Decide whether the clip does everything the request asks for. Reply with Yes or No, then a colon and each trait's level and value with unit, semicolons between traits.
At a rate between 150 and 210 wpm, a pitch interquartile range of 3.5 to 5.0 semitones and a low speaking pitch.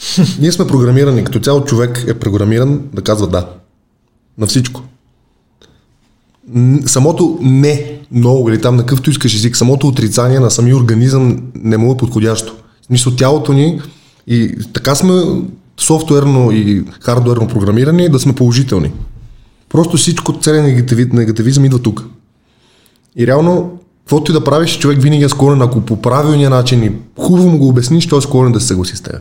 Yes: average, 160 wpm; average, 3.8 semitones; low, 125 Hz